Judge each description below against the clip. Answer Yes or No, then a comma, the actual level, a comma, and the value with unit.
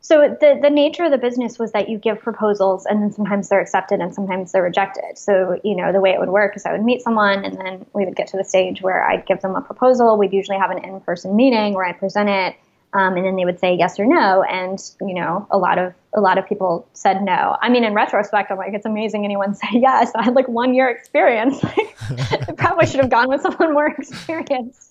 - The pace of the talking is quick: Yes, fast, 255 wpm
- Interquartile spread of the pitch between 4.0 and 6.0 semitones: Yes, average, 4.3 semitones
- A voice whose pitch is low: No, high, 205 Hz